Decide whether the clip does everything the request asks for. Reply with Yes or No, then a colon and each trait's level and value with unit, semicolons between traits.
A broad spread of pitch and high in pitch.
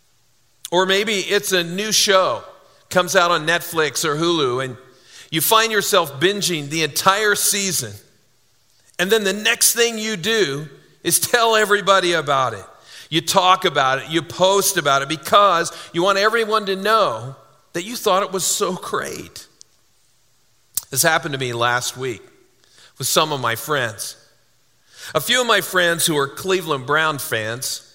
No: wide, 6.4 semitones; medium, 170 Hz